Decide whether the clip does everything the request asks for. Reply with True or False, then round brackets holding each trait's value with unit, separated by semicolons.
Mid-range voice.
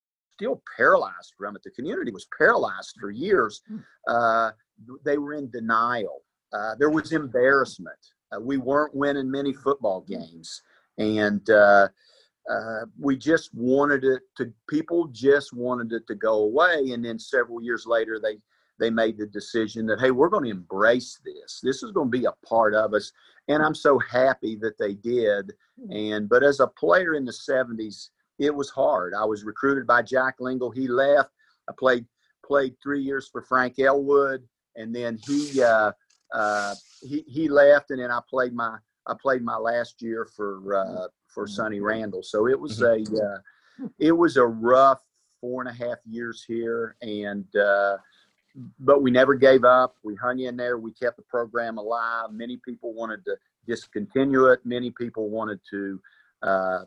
False (120 Hz)